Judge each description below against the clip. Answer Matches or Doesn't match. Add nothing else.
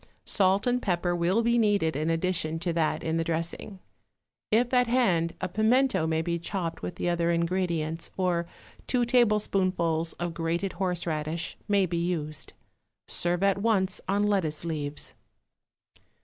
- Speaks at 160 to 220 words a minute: Doesn't match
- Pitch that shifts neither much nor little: Matches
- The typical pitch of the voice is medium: Matches